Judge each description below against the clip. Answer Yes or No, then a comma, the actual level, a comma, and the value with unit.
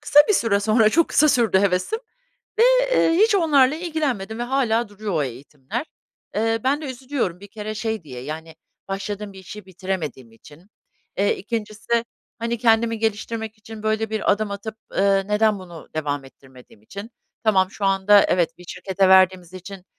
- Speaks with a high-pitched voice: Yes, high, 210 Hz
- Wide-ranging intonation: No, average, 3.5 semitones